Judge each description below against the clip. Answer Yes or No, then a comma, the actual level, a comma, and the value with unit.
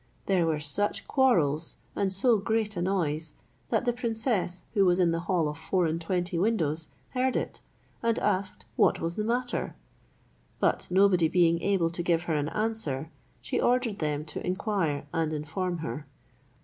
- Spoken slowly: No, average, 170 wpm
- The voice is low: No, medium, 180 Hz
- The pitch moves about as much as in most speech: Yes, average, 4.6 semitones